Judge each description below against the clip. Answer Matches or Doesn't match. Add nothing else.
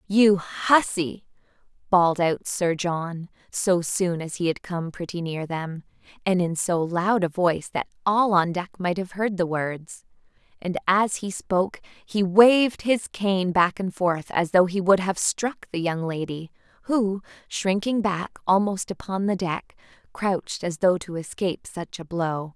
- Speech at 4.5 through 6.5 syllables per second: Doesn't match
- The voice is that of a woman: Matches